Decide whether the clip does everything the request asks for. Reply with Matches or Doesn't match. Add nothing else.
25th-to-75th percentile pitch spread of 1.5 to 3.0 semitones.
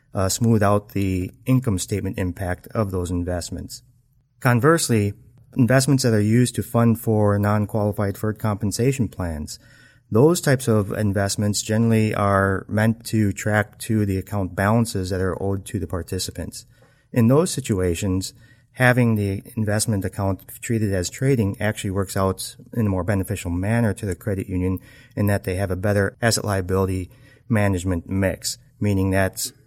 Doesn't match